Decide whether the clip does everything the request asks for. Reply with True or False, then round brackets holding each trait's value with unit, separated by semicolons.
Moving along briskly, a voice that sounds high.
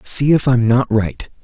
False (210 wpm; 120 Hz)